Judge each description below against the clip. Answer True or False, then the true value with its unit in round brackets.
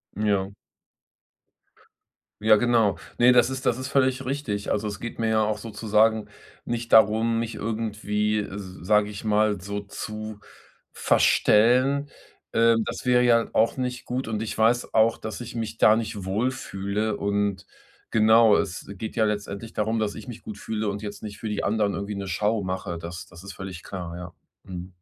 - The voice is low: True (110 Hz)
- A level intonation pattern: True (2.1 semitones)